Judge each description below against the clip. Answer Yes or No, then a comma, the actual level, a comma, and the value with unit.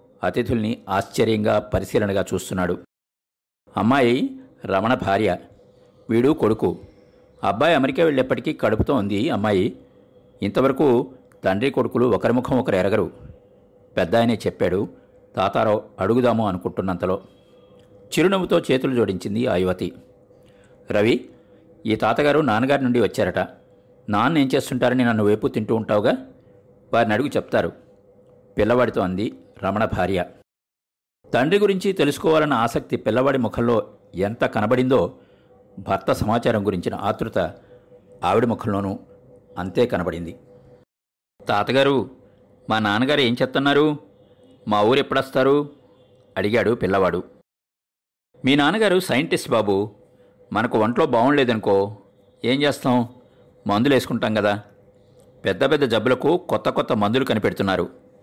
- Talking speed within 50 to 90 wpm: No, average, 100 wpm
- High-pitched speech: No, low, 115 Hz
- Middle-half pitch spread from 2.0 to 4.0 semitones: No, average, 4.4 semitones